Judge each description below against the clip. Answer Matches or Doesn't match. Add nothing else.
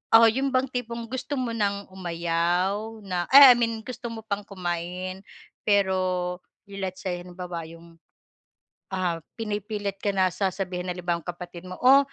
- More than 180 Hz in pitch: Matches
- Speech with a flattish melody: Doesn't match